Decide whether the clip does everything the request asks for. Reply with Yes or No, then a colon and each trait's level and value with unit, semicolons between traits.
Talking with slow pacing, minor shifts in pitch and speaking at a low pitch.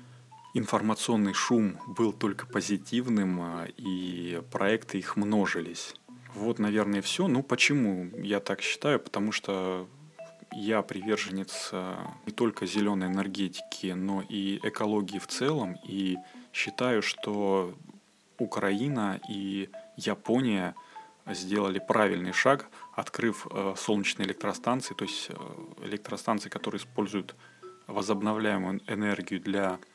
Yes: slow, 100 wpm; narrow, 2.1 semitones; low, 100 Hz